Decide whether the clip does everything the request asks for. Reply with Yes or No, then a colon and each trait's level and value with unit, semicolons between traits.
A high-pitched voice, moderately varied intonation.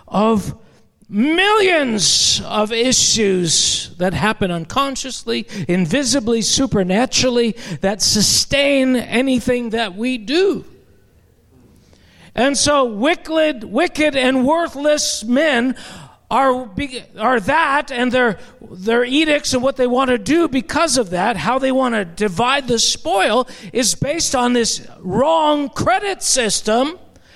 Yes: very high, 250 Hz; average, 4.5 semitones